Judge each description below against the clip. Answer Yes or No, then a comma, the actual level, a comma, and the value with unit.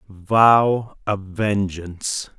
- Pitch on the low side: Yes, low, 100 Hz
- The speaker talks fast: No, slow, 75 wpm